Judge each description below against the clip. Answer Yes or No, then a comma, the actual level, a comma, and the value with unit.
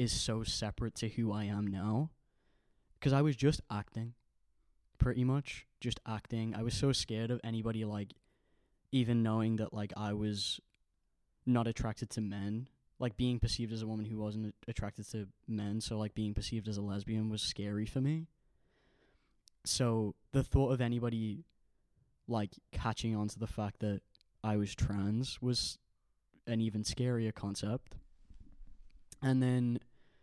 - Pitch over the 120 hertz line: No, low, 110 Hz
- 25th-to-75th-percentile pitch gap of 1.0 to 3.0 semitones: Yes, narrow, 2.6 semitones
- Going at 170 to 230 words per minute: No, average, 155 wpm